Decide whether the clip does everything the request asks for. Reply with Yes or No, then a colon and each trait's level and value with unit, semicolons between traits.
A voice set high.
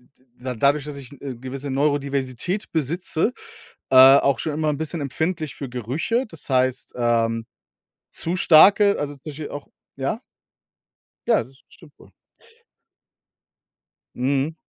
No: medium, 140 Hz